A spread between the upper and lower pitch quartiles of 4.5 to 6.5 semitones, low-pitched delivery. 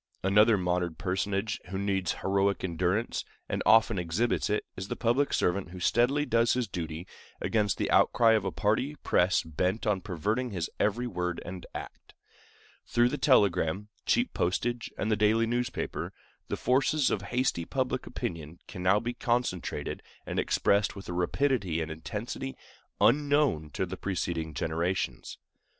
Yes: average, 4.8 semitones; low, 100 Hz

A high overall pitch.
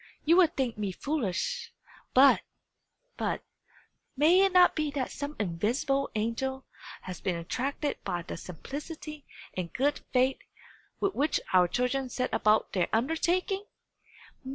Yes: very high, 270 Hz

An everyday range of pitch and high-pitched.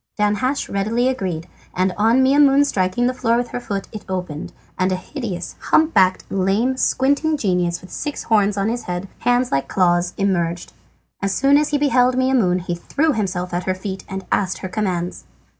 No: wide, 5.7 semitones; high, 200 Hz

